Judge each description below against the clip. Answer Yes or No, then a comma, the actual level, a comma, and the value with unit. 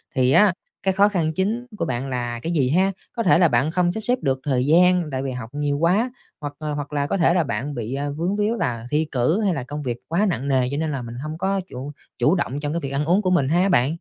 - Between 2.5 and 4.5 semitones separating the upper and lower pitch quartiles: No, average, 5.2 semitones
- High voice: No, medium, 150 Hz